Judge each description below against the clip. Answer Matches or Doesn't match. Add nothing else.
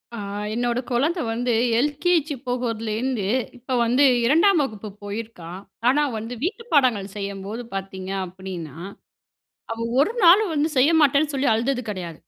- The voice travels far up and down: Matches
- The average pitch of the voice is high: Matches